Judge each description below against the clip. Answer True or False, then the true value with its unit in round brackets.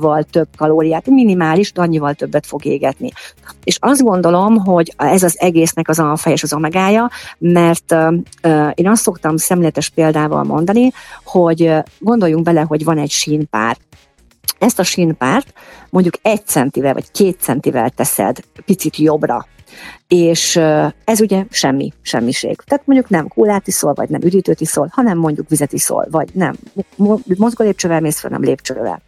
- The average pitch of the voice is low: False (170 Hz)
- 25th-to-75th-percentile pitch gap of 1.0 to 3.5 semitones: False (4.0 semitones)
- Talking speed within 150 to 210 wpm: True (155 wpm)